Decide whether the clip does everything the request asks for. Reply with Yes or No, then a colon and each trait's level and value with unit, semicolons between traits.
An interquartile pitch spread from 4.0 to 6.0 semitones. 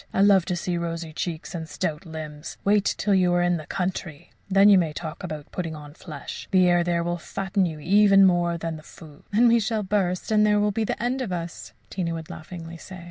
No: average, 3.2 semitones